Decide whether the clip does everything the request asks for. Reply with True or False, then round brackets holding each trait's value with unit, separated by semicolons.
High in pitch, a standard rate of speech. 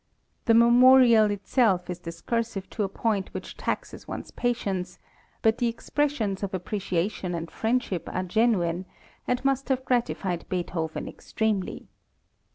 False (210 Hz; 130 wpm)